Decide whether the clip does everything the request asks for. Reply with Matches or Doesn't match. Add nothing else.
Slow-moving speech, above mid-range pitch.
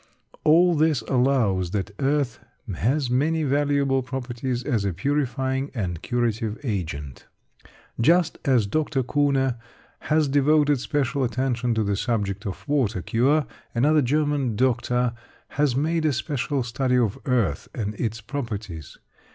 Doesn't match